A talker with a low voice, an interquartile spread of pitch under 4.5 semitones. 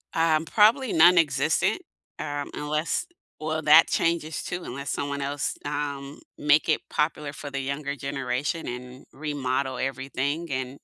No: medium, 145 Hz; narrow, 2.4 semitones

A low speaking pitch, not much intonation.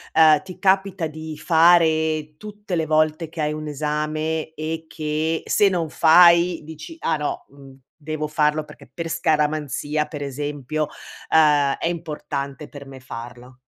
No: medium, 155 Hz; narrow, 1.5 semitones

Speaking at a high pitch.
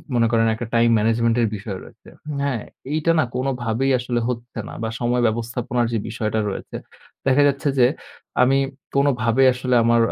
No: low, 120 Hz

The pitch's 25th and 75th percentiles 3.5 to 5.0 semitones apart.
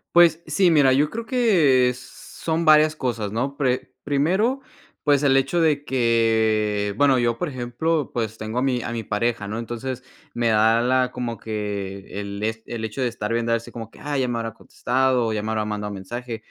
Yes: average, 4.0 semitones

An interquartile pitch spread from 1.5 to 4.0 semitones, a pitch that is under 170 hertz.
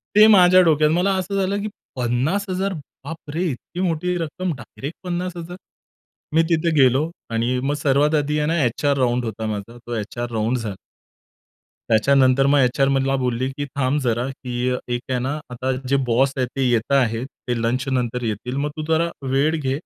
No: average, 4.8 semitones; low, 135 Hz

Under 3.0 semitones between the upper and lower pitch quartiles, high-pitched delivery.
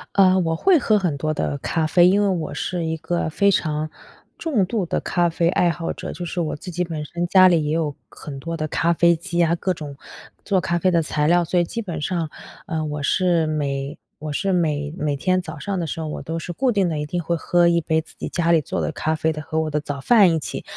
No: narrow, 2.6 semitones; medium, 165 Hz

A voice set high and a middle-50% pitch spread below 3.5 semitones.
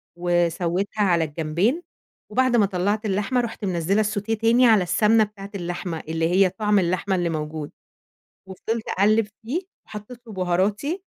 No: high, 200 Hz; average, 3.9 semitones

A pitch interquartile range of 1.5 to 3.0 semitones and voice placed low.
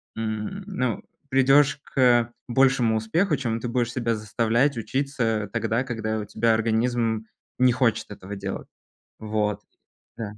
Yes: narrow, 2.6 semitones; low, 115 Hz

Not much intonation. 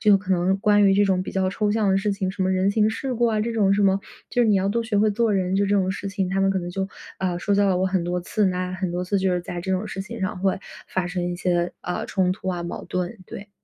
Yes: narrow, 2.0 semitones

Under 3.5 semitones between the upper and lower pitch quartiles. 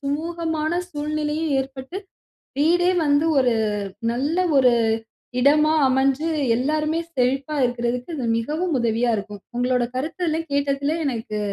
No: average, 3.8 semitones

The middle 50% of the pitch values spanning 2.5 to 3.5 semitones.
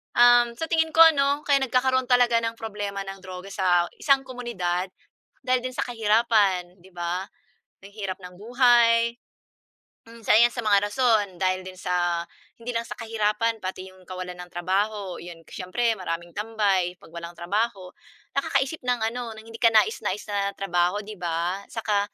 No: average, 4.4 semitones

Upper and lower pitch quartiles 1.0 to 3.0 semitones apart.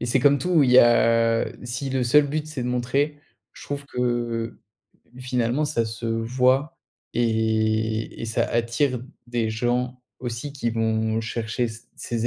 Yes: narrow, 2.4 semitones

